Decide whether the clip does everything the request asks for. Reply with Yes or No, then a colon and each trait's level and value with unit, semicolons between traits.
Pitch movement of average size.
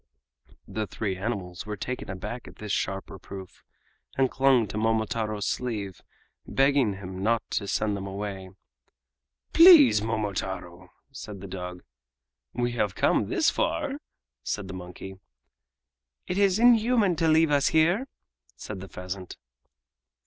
No: wide, 5.8 semitones